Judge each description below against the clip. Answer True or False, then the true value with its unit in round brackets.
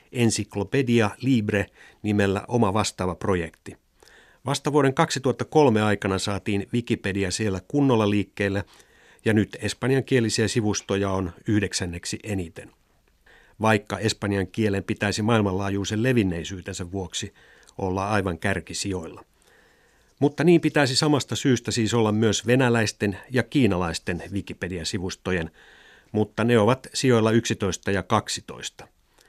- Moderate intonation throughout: True (3.4 semitones)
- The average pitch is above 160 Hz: False (105 Hz)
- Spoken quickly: False (105 wpm)